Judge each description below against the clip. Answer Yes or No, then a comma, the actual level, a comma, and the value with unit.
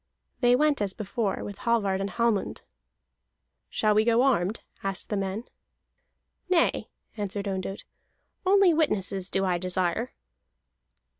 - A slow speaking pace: Yes, slow, 125 wpm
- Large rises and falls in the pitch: No, average, 3.7 semitones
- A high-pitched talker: Yes, high, 205 Hz